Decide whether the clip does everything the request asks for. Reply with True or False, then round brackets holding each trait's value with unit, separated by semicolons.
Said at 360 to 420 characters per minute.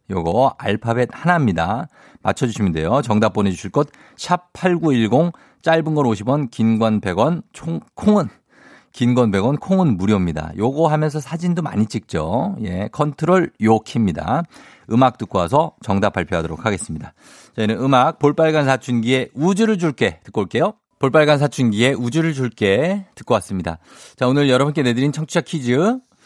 False (320 characters per minute)